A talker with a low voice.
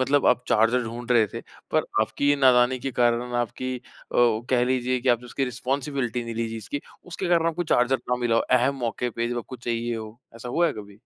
Yes: low, 120 Hz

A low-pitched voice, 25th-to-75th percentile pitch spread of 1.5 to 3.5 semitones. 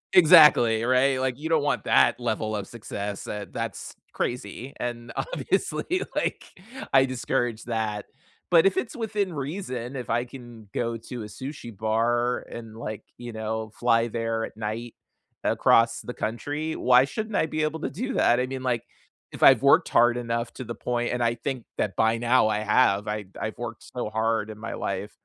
Yes: low, 120 Hz; average, 2.9 semitones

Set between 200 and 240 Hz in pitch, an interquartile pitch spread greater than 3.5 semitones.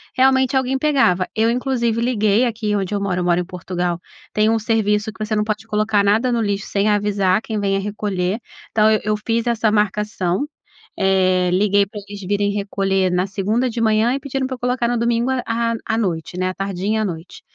No: high, 210 Hz; average, 2.9 semitones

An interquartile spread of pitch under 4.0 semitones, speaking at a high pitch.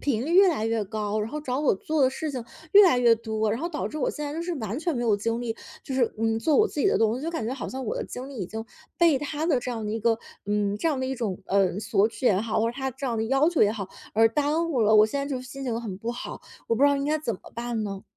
No: average, 4.7 semitones; high, 240 Hz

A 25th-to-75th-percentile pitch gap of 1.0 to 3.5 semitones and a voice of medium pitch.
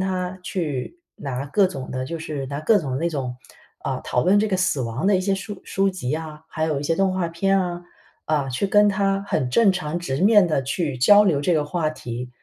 No: wide, 5.4 semitones; medium, 165 Hz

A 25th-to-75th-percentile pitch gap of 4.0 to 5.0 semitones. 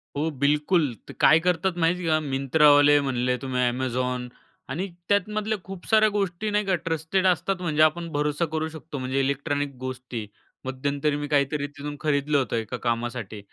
Yes: average, 4.3 semitones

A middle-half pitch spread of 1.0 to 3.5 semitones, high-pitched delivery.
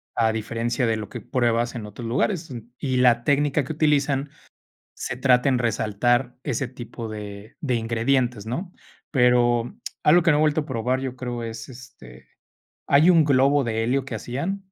No: average, 3.2 semitones; low, 125 Hz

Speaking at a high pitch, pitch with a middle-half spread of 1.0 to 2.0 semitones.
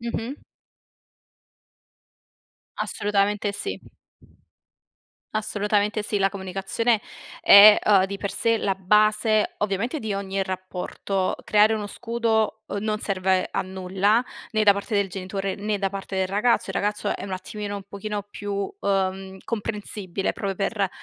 Yes: high, 205 Hz; narrow, 1.7 semitones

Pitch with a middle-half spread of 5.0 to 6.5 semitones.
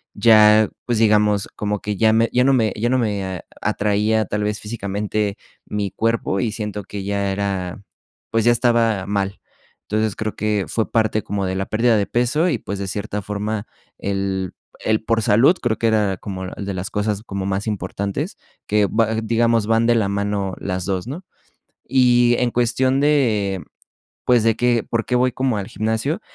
No: narrow, 2.5 semitones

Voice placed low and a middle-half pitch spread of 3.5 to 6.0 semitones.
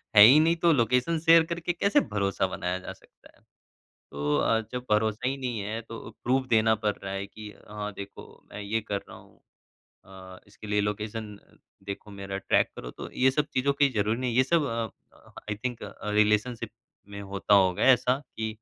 Yes: low, 110 Hz; average, 4.1 semitones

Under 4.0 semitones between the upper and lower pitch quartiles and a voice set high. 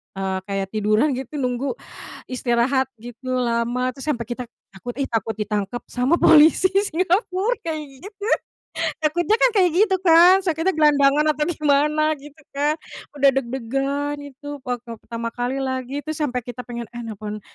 No: average, 4.3 semitones; very high, 270 Hz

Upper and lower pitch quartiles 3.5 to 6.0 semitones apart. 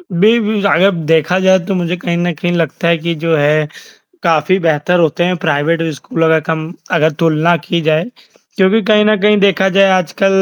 No: average, 2.9 semitones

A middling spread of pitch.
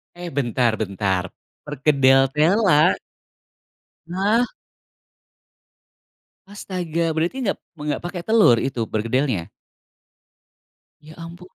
No: wide, 5.8 semitones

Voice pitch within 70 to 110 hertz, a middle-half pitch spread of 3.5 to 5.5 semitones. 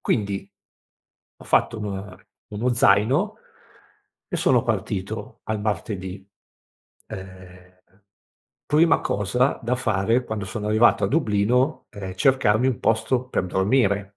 Yes: low, 105 Hz; average, 4.0 semitones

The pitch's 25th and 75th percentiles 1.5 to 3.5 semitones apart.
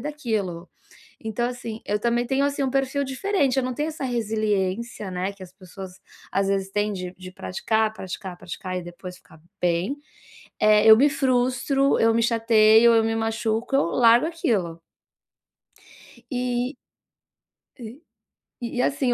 No: average, 4.6 semitones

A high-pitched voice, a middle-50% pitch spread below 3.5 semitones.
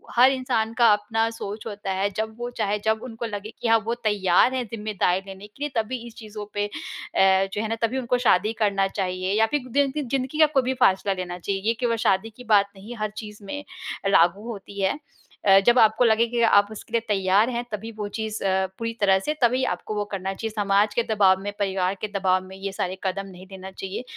Yes: high, 210 Hz; average, 2.9 semitones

